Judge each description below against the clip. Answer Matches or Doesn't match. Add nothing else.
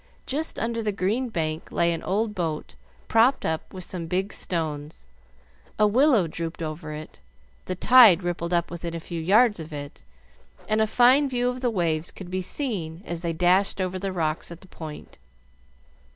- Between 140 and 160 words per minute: Doesn't match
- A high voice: Doesn't match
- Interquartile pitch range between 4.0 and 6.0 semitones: Matches